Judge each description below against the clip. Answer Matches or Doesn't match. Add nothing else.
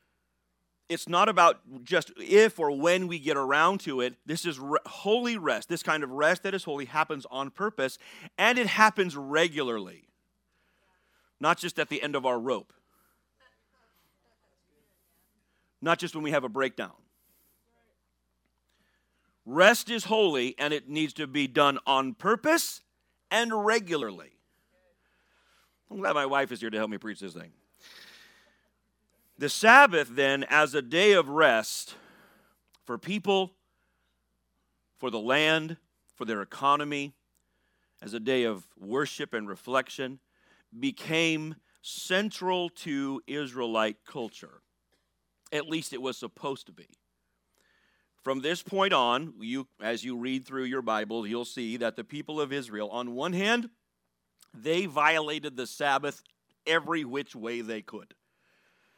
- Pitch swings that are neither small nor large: Doesn't match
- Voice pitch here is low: Doesn't match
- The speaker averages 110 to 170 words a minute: Matches